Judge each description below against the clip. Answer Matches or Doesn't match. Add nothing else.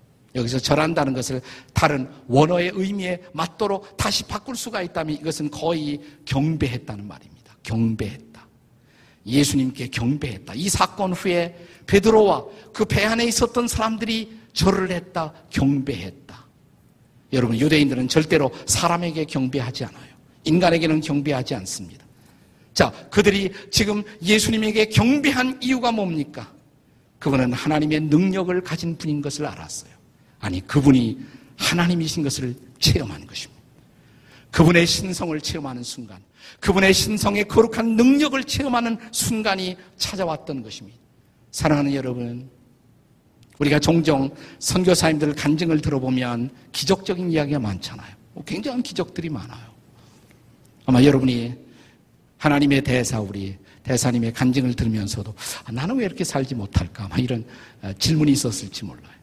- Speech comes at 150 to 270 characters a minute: Doesn't match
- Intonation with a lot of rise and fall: Matches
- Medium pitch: Matches